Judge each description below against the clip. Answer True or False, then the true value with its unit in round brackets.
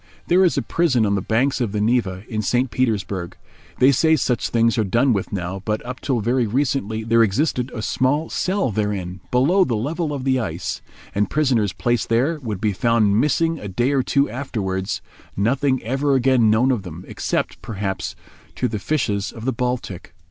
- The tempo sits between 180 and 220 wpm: True (190 wpm)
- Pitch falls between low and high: False (120 Hz)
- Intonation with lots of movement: False (4.4 semitones)